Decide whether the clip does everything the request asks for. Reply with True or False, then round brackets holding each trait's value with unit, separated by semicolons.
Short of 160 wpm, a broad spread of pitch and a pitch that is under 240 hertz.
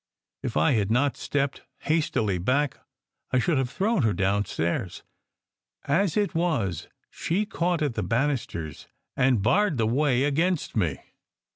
True (145 wpm; 7.5 semitones; 135 Hz)